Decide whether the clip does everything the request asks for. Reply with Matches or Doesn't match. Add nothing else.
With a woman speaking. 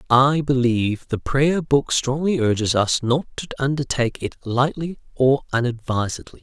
Doesn't match